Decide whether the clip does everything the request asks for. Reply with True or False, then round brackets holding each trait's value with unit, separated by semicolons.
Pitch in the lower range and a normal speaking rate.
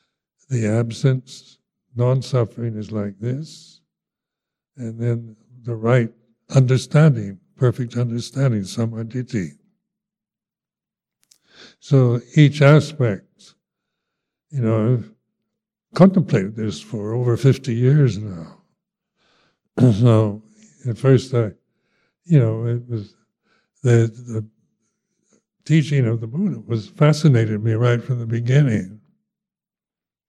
False (125 Hz; 95 wpm)